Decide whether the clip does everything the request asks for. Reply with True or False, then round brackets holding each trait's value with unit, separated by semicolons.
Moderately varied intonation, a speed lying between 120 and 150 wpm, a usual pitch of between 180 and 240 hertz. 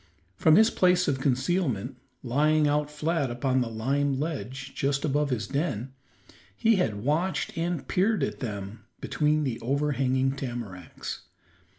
False (3.5 semitones; 135 wpm; 140 Hz)